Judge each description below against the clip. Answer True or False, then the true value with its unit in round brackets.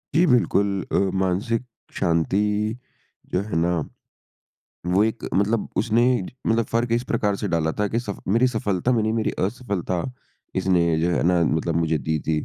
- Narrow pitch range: False (4.5 semitones)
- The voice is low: True (100 Hz)